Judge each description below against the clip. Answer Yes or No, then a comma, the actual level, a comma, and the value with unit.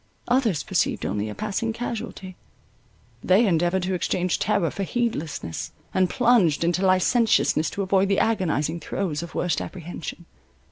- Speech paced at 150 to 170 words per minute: No, average, 140 wpm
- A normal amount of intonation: Yes, average, 4.0 semitones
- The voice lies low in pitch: No, medium, 185 Hz